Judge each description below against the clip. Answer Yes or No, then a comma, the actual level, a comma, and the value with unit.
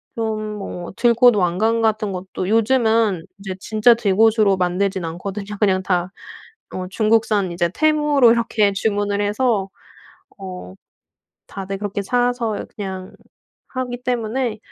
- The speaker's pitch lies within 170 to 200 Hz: No, high, 210 Hz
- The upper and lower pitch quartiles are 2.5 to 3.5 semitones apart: Yes, average, 3.2 semitones